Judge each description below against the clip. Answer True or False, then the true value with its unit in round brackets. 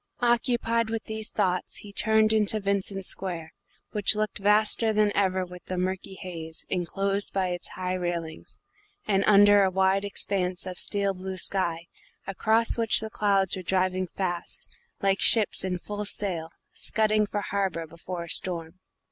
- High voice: True (195 Hz)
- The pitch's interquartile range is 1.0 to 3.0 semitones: True (2.4 semitones)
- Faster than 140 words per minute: True (155 wpm)